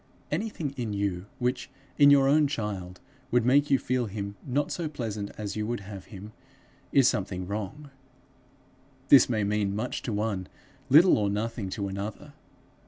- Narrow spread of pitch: No, average, 5.0 semitones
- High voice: No, low, 110 Hz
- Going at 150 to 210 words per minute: Yes, average, 165 wpm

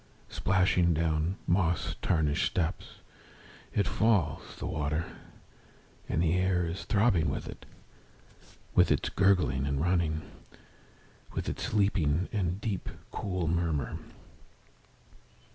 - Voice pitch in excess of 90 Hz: No, very low, 85 Hz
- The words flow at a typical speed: No, slow, 110 wpm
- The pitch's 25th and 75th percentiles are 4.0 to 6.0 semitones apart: No, average, 3.3 semitones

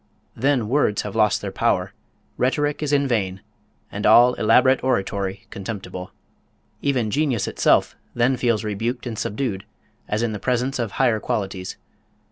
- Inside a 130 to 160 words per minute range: Yes, average, 145 wpm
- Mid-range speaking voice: No, low, 115 Hz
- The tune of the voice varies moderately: Yes, average, 4.1 semitones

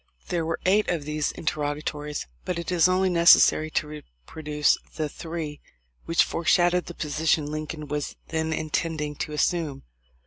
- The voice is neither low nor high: Yes, medium, 155 Hz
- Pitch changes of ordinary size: No, narrow, 2.1 semitones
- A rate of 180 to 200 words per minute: No, average, 150 wpm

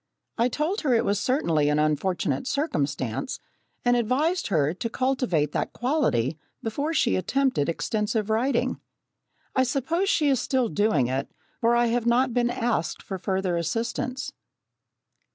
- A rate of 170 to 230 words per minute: No, average, 145 wpm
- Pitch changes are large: Yes, wide, 7.2 semitones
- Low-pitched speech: No, high, 230 Hz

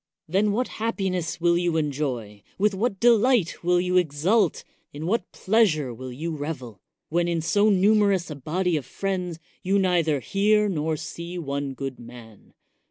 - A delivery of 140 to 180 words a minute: Yes, average, 160 wpm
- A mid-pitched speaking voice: Yes, medium, 175 Hz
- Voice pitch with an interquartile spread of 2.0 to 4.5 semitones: No, average, 5.1 semitones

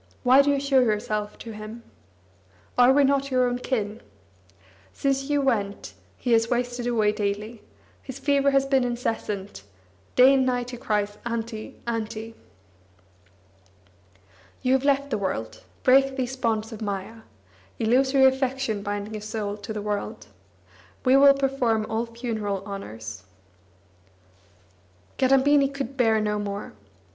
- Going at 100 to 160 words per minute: Yes, slow, 135 wpm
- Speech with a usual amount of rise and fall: Yes, average, 4.0 semitones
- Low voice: No, high, 235 Hz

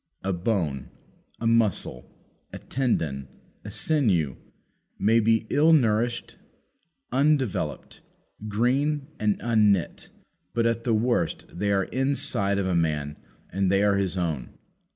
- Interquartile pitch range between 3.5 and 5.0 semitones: Yes, average, 4.6 semitones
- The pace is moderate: No, slow, 125 wpm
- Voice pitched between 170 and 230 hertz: No, low, 105 Hz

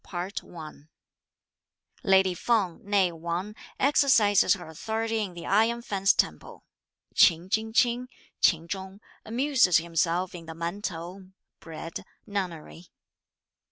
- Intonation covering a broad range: No, average, 4.0 semitones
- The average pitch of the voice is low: No, high, 190 Hz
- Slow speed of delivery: Yes, slow, 120 wpm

